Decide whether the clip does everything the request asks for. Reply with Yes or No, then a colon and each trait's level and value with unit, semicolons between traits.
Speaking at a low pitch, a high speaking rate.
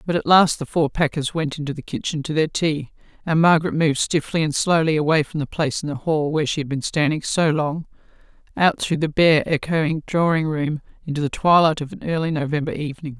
No: medium, 155 Hz; fast, 220 wpm